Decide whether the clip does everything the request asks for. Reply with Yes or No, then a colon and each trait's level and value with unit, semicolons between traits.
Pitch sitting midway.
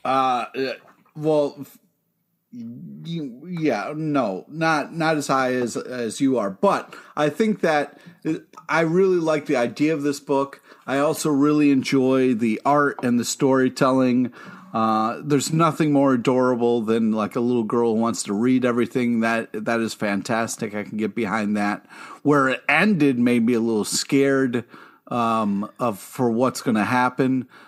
No: low, 130 Hz